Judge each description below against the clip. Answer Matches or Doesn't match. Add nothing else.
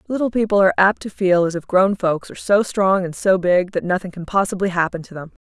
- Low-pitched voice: Doesn't match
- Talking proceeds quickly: Matches